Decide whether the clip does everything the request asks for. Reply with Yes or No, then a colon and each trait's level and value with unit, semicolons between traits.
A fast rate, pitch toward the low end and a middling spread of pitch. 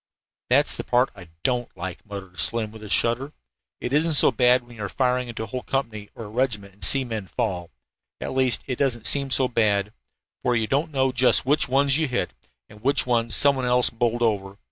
Yes: fast, 225 wpm; low, 120 Hz; average, 3.7 semitones